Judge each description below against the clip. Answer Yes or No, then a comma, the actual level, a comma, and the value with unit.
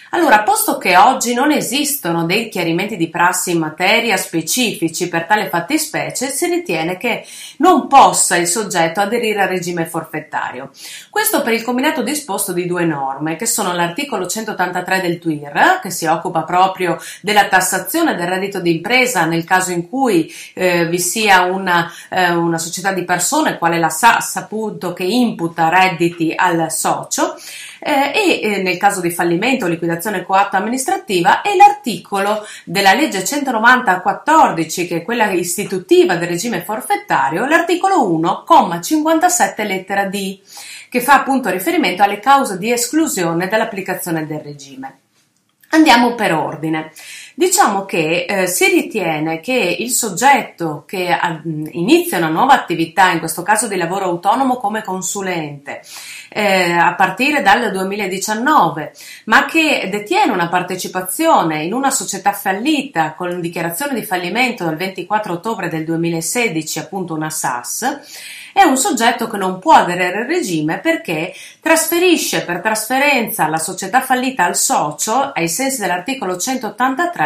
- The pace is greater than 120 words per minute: Yes, average, 140 wpm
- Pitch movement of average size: No, wide, 6.7 semitones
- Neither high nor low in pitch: No, high, 195 Hz